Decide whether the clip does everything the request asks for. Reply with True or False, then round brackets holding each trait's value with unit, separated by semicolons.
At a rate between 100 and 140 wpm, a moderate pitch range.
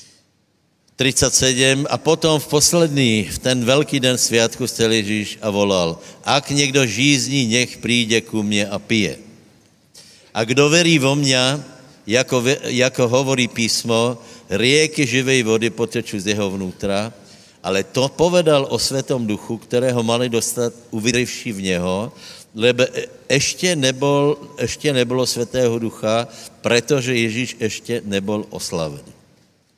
True (125 wpm; 3.2 semitones)